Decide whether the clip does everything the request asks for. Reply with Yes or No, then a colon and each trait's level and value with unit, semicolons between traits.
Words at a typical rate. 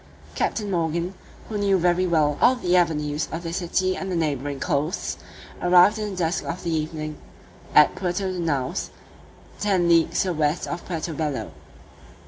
Yes: average, 170 wpm